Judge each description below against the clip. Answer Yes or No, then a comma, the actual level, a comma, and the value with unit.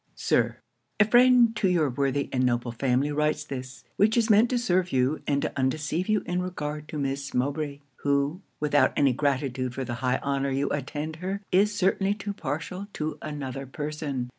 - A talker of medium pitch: Yes, medium, 150 Hz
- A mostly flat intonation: No, average, 5.2 semitones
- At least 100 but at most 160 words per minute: No, average, 185 wpm